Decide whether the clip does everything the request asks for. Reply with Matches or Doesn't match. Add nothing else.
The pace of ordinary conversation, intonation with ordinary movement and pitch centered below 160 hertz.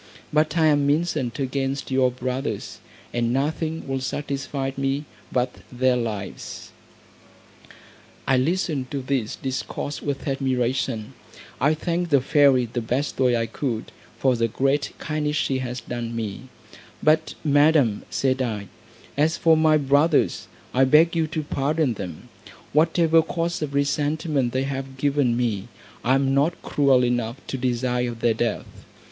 Matches